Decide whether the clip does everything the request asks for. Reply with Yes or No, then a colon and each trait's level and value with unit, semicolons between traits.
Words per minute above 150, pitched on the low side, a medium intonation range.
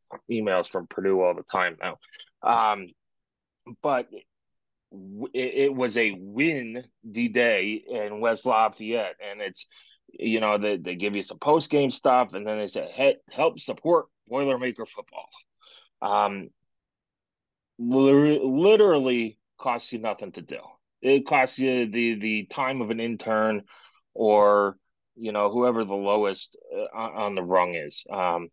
No: slow, 135 wpm; low, 115 Hz; average, 4.0 semitones